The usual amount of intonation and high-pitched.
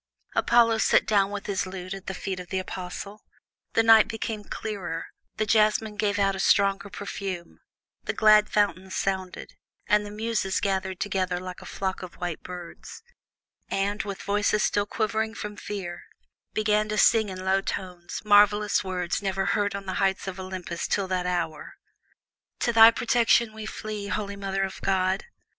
No: narrow, 2.1 semitones; high, 200 Hz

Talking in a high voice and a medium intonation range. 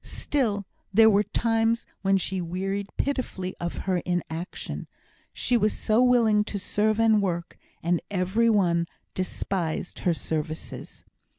Yes: high, 195 Hz; average, 3.8 semitones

